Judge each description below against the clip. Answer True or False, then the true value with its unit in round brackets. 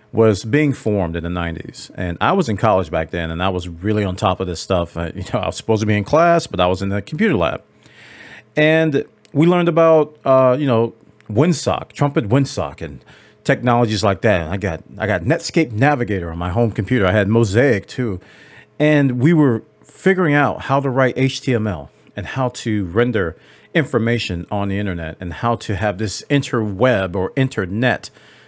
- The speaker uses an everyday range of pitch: False (6.1 semitones)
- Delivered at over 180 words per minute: True (195 wpm)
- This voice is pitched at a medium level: False (110 Hz)